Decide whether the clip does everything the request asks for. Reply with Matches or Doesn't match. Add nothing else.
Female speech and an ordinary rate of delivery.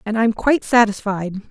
Matches